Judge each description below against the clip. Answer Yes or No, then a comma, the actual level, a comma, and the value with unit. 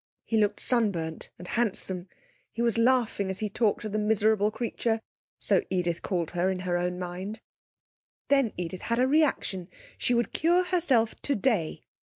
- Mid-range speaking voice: No, high, 215 Hz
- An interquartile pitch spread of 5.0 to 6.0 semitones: No, average, 4.6 semitones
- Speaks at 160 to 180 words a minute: Yes, average, 165 wpm